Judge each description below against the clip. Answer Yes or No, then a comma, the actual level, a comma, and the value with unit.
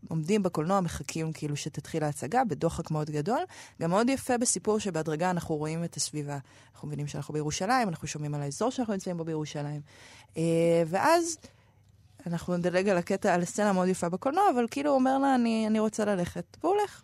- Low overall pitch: No, medium, 175 Hz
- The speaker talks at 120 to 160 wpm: No, fast, 180 wpm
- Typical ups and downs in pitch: No, wide, 6.0 semitones